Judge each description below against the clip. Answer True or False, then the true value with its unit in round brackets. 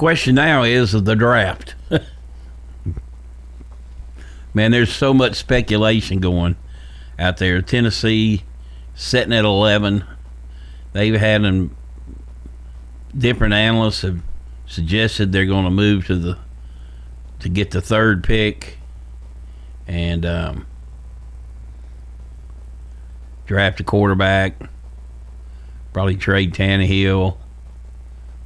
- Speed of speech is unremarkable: False (95 wpm)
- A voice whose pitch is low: True (80 Hz)